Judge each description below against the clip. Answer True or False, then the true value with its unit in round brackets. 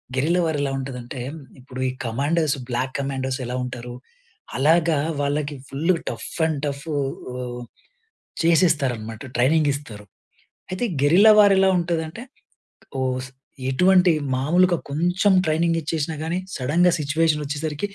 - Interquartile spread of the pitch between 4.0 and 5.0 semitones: True (4.3 semitones)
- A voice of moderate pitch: True (150 Hz)